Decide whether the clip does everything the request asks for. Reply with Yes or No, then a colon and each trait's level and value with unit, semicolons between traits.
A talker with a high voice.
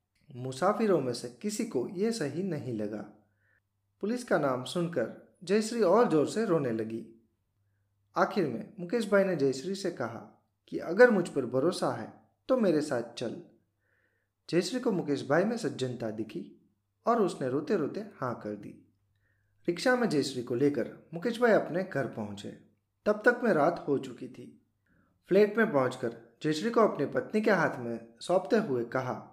No: medium, 140 Hz